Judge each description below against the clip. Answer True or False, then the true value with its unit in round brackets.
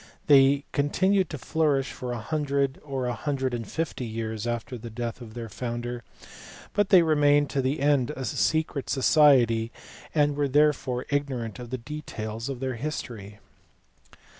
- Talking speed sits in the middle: True (165 wpm)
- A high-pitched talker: False (135 Hz)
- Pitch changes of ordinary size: True (3.6 semitones)